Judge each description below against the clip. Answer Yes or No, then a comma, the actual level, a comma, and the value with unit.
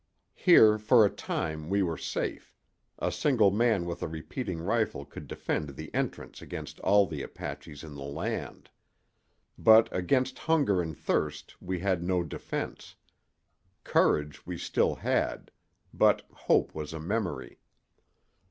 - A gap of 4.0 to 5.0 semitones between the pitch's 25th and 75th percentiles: No, wide, 5.6 semitones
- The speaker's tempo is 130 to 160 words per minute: Yes, average, 140 wpm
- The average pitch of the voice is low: Yes, very low, 90 Hz